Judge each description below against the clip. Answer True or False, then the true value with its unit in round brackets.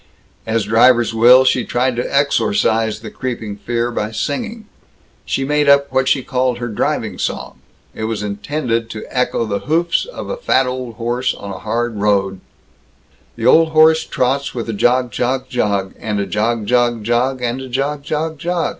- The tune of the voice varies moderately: True (3.5 semitones)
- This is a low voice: True (125 Hz)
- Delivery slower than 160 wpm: False (180 wpm)